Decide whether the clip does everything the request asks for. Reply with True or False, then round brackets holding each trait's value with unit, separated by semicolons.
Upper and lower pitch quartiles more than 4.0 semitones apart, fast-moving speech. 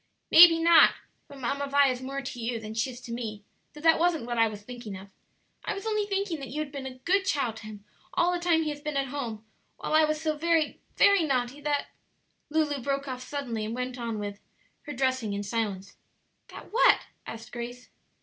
True (4.9 semitones; 225 wpm)